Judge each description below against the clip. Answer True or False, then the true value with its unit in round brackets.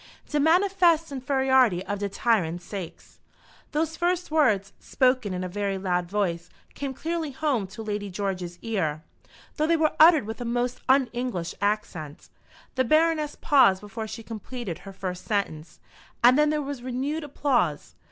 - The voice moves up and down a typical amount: False (7.1 semitones)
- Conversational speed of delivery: True (160 wpm)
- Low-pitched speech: False (235 Hz)